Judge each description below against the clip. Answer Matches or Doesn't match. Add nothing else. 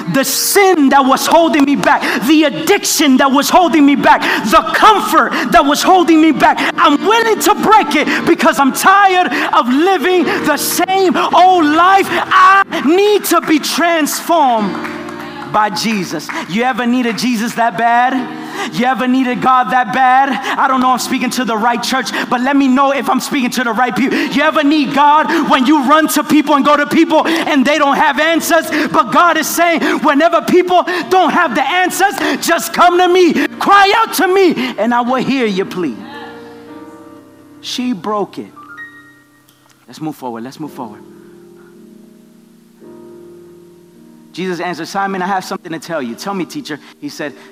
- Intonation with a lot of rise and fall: Matches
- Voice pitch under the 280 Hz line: Doesn't match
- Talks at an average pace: Matches